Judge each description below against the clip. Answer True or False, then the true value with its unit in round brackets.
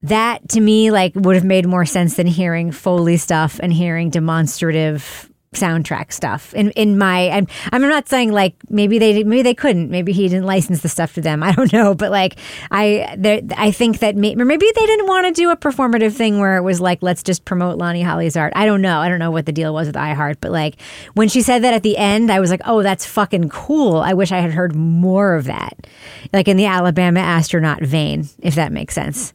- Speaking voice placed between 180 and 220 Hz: True (185 Hz)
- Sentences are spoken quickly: True (235 wpm)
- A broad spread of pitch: False (4.1 semitones)